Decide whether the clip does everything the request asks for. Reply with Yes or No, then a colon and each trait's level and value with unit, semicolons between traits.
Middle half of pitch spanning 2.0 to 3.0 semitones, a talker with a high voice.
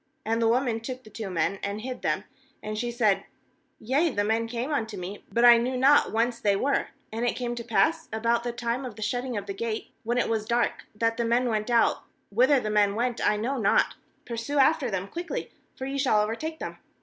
Yes: average, 2.7 semitones; high, 235 Hz